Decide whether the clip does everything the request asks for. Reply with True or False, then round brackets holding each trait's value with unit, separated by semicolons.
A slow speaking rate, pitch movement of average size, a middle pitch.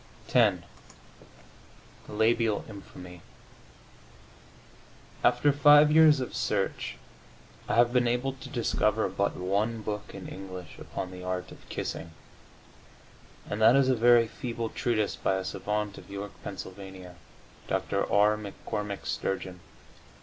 False (125 wpm; 3.6 semitones; 105 Hz)